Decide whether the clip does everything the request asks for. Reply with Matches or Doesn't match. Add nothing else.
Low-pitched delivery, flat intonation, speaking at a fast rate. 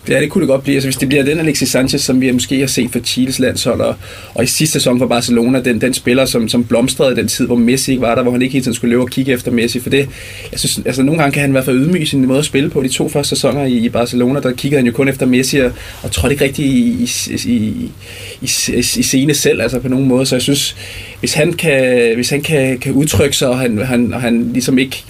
Matches